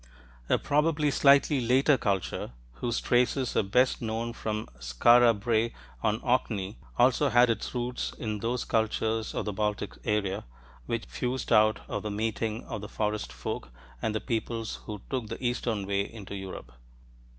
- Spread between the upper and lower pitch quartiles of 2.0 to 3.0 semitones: Yes, average, 2.7 semitones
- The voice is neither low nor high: No, low, 115 Hz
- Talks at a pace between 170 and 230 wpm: No, average, 160 wpm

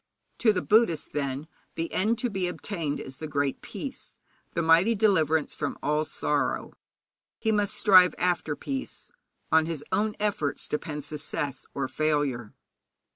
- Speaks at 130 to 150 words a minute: Yes, average, 145 wpm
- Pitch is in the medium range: Yes, medium, 160 Hz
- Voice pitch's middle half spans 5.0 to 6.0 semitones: Yes, wide, 5.4 semitones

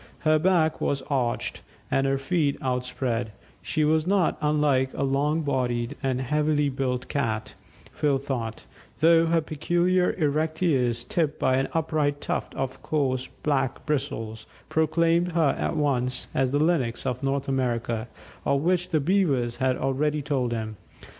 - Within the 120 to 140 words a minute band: No, average, 150 wpm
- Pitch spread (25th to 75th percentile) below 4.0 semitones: Yes, average, 3.4 semitones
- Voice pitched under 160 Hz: Yes, medium, 140 Hz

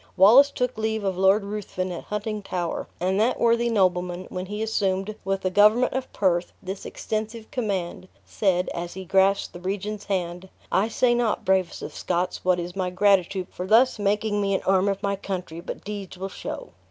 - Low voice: No, high, 195 Hz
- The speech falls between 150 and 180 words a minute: No, average, 190 wpm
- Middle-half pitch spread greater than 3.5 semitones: No, narrow, 2.5 semitones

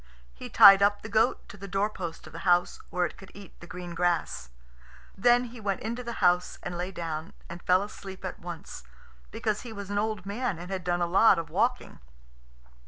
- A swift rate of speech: Yes, fast, 210 wpm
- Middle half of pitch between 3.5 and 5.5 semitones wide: No, average, 2.9 semitones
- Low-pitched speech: No, high, 190 Hz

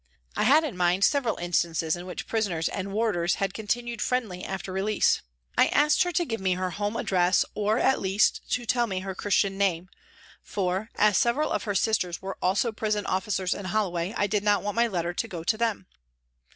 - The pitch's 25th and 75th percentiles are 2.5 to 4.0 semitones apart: Yes, average, 3.4 semitones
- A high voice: Yes, high, 200 Hz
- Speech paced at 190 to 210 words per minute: Yes, fast, 205 wpm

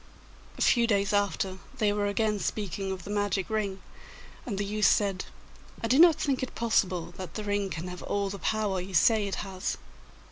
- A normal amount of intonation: No, narrow, 2.1 semitones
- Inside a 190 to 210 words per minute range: Yes, average, 200 wpm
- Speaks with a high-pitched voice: Yes, high, 205 Hz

